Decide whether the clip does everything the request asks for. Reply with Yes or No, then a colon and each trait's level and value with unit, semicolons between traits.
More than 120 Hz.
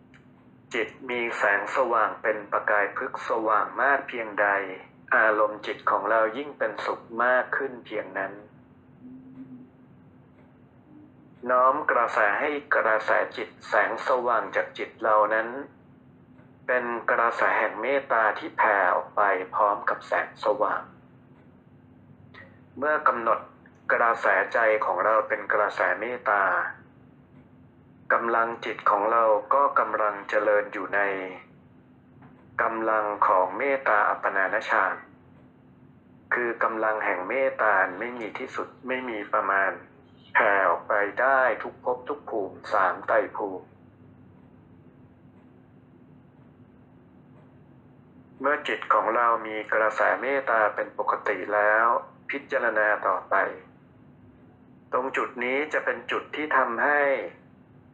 No: low, 110 Hz